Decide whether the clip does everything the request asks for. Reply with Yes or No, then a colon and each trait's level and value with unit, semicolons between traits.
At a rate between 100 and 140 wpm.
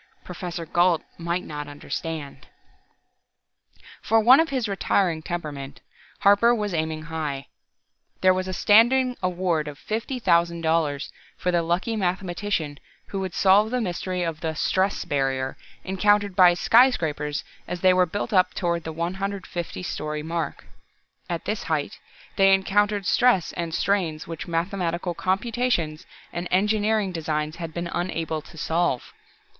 Yes: slow, 135 wpm